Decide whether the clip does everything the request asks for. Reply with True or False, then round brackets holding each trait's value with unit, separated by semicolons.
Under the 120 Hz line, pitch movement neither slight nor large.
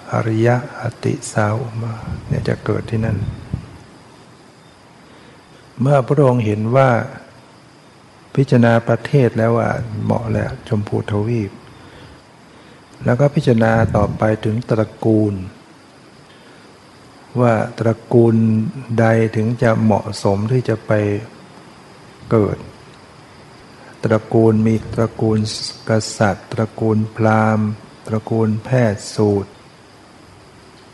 False (110 Hz; 1.9 semitones)